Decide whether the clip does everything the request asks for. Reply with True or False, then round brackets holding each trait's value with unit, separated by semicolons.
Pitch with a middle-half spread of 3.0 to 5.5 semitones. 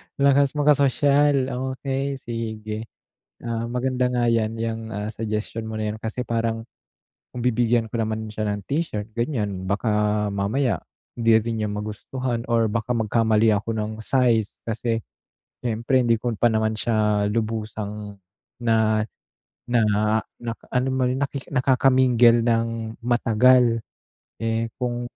False (2.4 semitones)